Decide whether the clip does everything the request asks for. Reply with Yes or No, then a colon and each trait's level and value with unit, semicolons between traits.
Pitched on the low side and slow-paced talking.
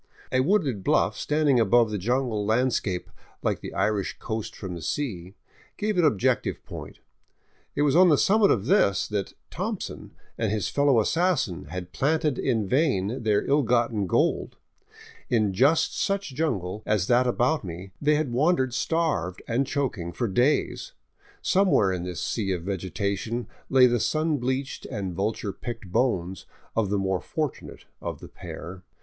No: low, 120 Hz; average, 165 wpm